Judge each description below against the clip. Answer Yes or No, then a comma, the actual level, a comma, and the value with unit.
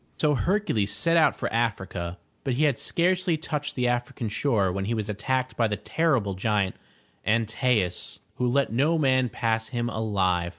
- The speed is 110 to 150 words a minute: No, average, 175 wpm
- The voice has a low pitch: Yes, low, 120 Hz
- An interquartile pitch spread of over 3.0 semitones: Yes, average, 5.2 semitones